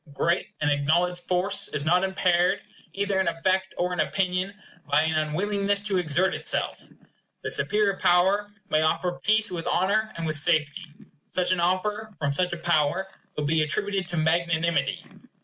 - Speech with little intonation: No, average, 3.2 semitones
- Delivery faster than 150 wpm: Yes, average, 165 wpm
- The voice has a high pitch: No, medium, 180 Hz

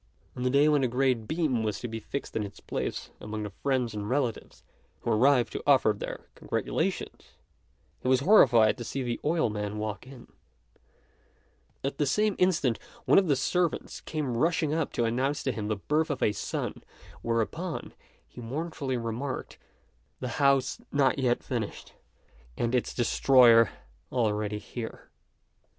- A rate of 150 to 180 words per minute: Yes, average, 160 wpm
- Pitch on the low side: Yes, low, 125 Hz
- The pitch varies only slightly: No, average, 3.9 semitones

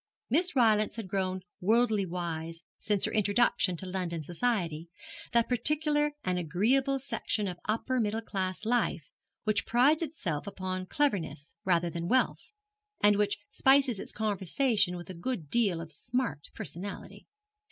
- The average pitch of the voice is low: No, high, 205 Hz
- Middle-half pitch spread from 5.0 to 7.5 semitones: Yes, wide, 5.6 semitones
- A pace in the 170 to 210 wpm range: No, average, 140 wpm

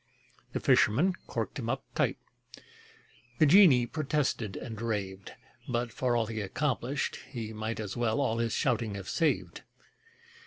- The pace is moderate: Yes, average, 145 wpm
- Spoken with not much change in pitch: No, average, 4.2 semitones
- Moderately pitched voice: No, low, 115 Hz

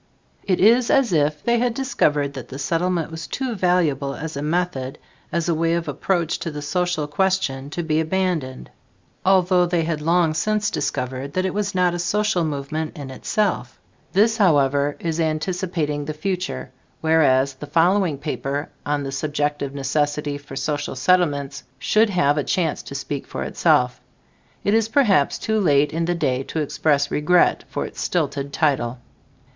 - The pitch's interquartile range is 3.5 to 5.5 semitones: Yes, average, 4.2 semitones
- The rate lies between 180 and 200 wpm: No, average, 165 wpm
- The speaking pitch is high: No, medium, 160 Hz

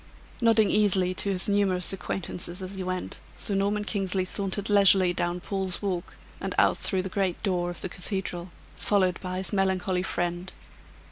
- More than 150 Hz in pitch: Yes, high, 190 Hz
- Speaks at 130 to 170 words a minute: Yes, average, 165 wpm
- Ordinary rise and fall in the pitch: No, narrow, 1.6 semitones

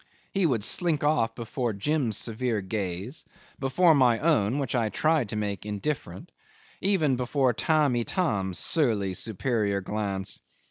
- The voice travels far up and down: Yes, wide, 6.3 semitones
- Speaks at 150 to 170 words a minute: No, slow, 135 wpm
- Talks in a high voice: No, low, 120 Hz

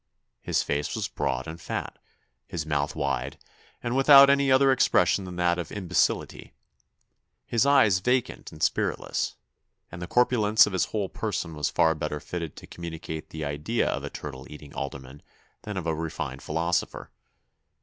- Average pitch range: No, wide, 6.2 semitones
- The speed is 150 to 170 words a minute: Yes, average, 160 wpm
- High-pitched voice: No, very low, 85 Hz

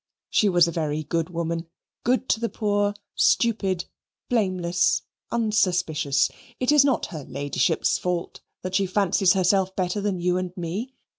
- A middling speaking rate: Yes, average, 150 wpm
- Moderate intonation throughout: Yes, average, 3.4 semitones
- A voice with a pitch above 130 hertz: Yes, medium, 185 Hz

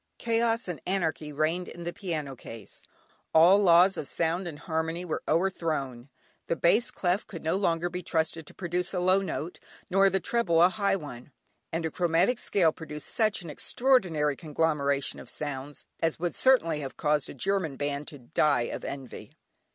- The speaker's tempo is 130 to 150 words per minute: No, average, 175 wpm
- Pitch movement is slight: No, average, 3.8 semitones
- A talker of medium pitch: Yes, medium, 165 Hz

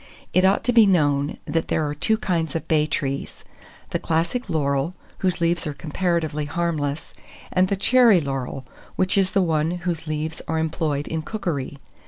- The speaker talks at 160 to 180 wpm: Yes, average, 175 wpm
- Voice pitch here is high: No, medium, 160 Hz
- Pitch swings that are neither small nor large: Yes, average, 3.6 semitones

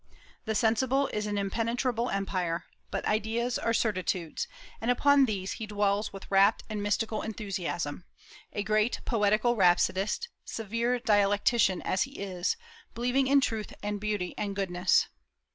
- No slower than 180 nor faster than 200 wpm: No, average, 140 wpm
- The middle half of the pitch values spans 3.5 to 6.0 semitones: No, average, 3.0 semitones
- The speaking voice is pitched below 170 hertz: No, high, 210 Hz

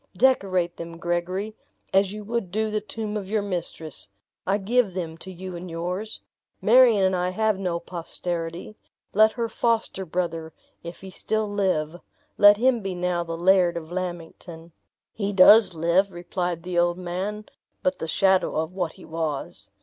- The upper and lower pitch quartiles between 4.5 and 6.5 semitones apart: No, average, 3.3 semitones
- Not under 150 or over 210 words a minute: Yes, average, 165 wpm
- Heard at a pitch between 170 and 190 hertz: Yes, medium, 185 Hz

